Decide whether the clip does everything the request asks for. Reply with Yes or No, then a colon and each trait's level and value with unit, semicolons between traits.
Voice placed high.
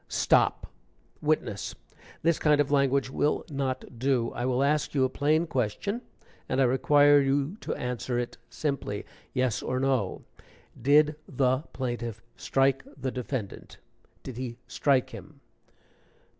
No: low, 135 Hz